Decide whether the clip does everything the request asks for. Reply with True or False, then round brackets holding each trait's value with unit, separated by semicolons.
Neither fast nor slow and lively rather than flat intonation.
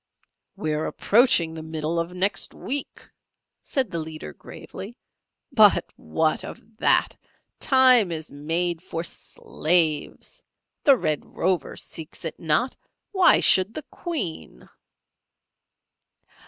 False (115 wpm; 6.0 semitones)